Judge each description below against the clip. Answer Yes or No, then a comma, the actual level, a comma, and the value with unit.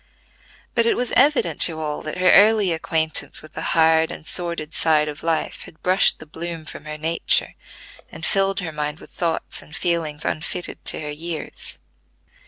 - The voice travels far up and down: No, narrow, 2.5 semitones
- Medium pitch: Yes, medium, 160 Hz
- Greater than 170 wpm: Yes, average, 180 wpm